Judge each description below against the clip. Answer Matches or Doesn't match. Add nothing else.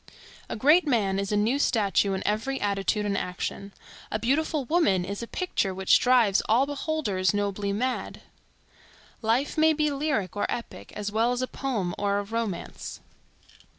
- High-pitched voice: Matches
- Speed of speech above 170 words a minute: Doesn't match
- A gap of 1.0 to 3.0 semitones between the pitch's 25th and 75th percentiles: Doesn't match